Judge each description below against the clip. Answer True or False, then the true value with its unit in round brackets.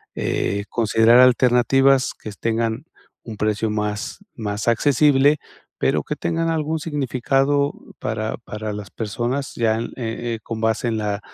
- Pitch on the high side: False (120 Hz)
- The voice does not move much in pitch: False (3.7 semitones)